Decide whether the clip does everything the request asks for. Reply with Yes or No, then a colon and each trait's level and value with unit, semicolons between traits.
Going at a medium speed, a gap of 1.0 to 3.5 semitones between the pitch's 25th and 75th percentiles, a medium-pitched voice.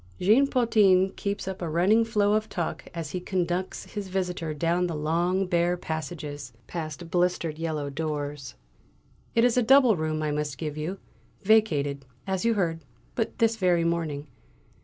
No: average, 160 wpm; average, 4.2 semitones; medium, 175 Hz